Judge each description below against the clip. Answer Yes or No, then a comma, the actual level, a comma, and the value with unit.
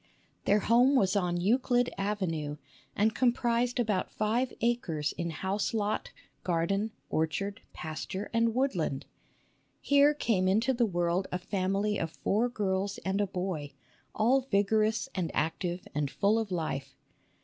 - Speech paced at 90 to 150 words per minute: Yes, average, 140 wpm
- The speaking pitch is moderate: No, high, 200 Hz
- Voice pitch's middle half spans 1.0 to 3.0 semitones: No, average, 4.5 semitones